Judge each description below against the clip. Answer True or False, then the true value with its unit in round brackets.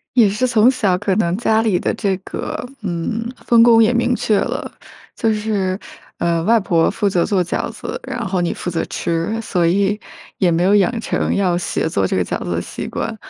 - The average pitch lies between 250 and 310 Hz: False (200 Hz)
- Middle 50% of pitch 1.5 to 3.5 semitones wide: False (4.4 semitones)